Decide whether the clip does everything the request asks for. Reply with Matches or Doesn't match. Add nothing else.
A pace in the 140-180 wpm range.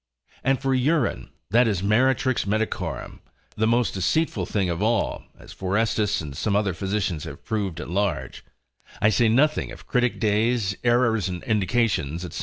Matches